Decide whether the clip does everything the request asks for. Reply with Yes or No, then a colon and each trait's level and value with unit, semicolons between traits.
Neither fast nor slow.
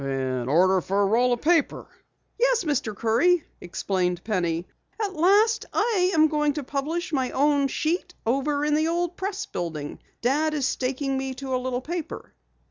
Yes: average, 170 wpm